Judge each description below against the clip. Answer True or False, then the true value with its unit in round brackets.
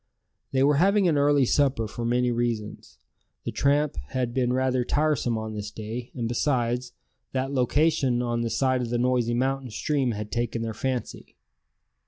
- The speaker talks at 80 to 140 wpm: False (170 wpm)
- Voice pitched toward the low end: True (125 Hz)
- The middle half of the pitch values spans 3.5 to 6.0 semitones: False (2.5 semitones)